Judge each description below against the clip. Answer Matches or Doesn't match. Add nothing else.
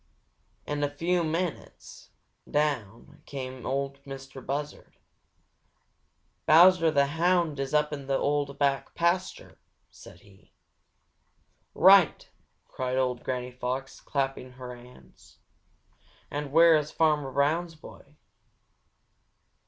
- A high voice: Doesn't match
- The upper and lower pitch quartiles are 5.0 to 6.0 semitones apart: Doesn't match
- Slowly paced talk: Matches